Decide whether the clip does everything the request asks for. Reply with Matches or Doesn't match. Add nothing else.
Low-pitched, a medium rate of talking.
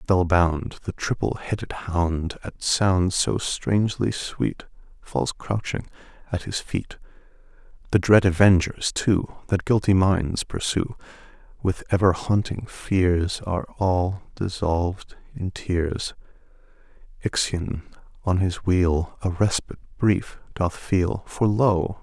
Doesn't match